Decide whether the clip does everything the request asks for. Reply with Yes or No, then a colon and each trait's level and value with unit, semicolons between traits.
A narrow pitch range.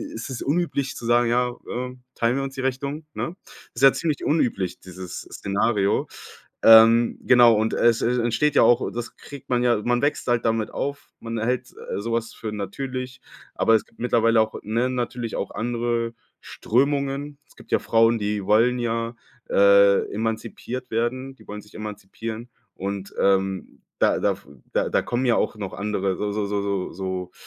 No: average, 3.1 semitones